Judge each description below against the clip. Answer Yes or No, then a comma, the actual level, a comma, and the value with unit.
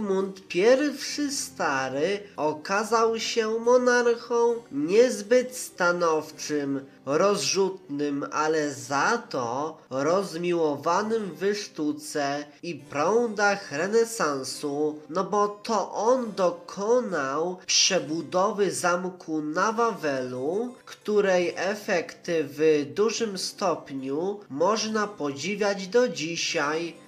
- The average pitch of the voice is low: No, high, 190 Hz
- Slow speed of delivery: Yes, slow, 80 wpm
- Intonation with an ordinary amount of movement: No, wide, 6.4 semitones